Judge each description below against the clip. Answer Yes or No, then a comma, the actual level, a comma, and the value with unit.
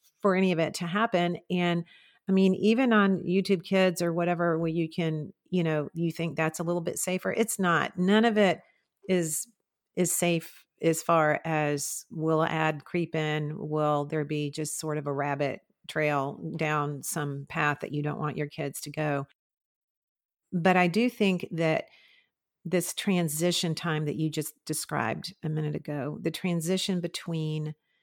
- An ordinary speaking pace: Yes, average, 170 wpm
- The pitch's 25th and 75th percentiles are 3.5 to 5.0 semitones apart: No, average, 3.1 semitones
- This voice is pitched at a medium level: Yes, medium, 165 Hz